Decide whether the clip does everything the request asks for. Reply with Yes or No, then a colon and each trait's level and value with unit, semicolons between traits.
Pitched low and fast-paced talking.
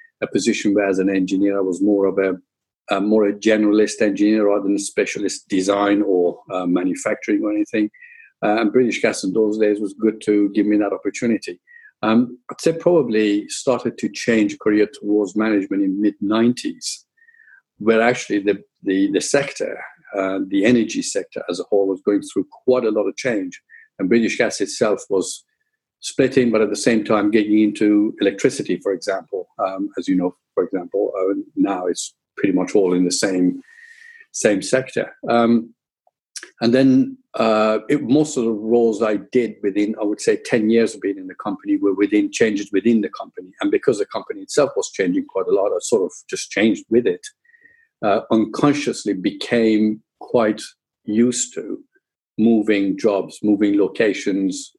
No: low, 115 Hz; average, 175 wpm